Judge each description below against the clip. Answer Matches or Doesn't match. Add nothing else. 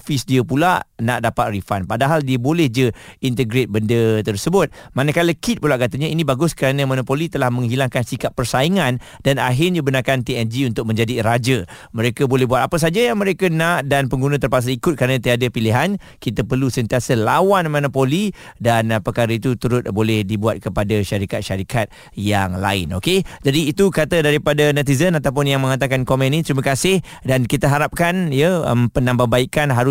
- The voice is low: Matches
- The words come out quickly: Matches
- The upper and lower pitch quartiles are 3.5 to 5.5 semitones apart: Matches